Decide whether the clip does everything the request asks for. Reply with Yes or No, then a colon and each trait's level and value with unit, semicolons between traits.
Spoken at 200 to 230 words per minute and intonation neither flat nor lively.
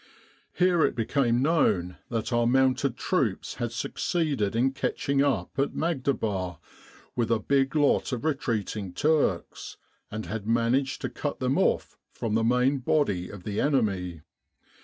No: average, 145 wpm; average, 4.7 semitones